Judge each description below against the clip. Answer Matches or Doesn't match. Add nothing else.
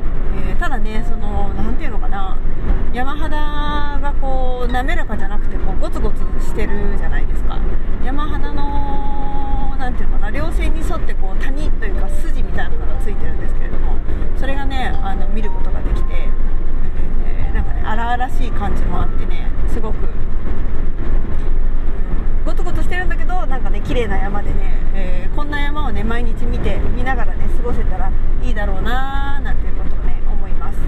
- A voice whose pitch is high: Doesn't match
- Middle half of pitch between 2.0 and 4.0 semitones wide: Doesn't match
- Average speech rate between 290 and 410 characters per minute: Matches